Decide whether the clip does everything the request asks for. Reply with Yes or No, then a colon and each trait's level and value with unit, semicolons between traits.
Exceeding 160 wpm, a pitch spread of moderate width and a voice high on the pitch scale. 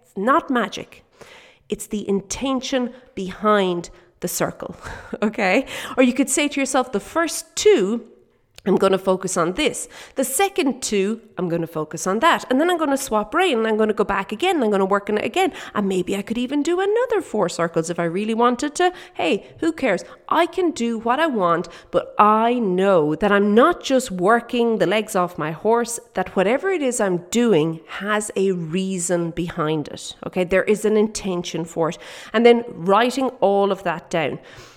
No: average, 200 wpm; wide, 5.9 semitones; high, 215 Hz